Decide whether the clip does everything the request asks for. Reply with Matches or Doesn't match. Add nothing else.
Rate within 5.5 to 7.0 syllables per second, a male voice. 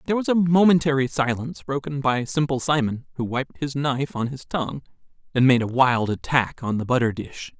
Matches